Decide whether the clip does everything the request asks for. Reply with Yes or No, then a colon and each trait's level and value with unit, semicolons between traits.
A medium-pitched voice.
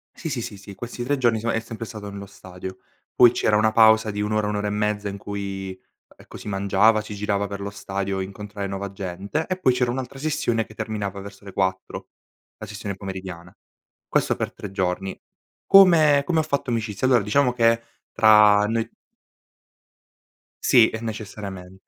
No: low, 105 Hz